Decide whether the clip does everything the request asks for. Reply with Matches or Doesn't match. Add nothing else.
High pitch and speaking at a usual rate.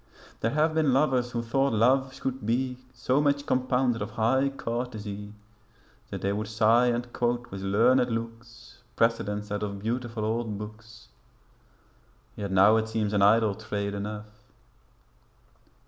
Doesn't match